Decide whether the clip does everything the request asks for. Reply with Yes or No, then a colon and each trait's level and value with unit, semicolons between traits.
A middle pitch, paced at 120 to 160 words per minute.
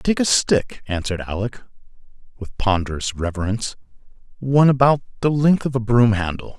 No: low, 115 Hz; average, 145 wpm